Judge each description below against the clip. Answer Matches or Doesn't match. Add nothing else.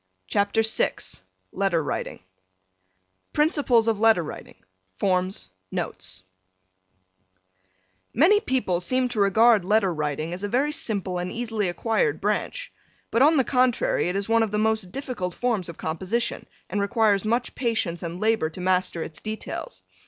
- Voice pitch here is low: Doesn't match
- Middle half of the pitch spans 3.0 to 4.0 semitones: Doesn't match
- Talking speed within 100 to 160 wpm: Matches